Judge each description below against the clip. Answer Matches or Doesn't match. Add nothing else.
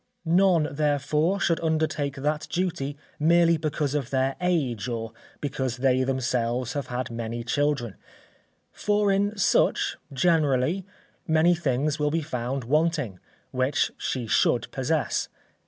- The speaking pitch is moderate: Matches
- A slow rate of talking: Matches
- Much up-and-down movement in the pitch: Doesn't match